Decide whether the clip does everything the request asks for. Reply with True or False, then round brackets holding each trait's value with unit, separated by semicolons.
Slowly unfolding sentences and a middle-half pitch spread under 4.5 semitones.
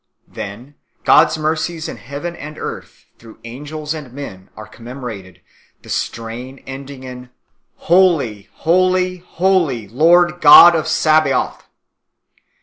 False (130 wpm; 5.5 semitones)